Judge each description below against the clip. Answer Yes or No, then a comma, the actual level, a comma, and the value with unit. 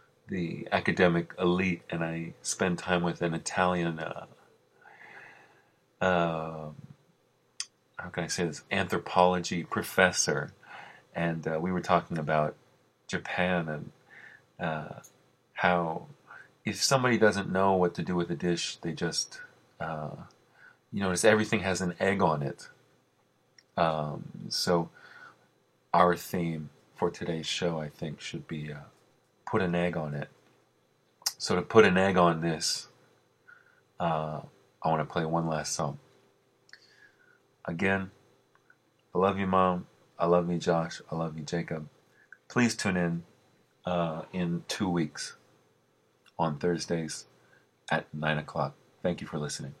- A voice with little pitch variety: Yes, narrow, 2.3 semitones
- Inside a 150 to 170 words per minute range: No, slow, 135 wpm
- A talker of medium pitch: No, very low, 85 Hz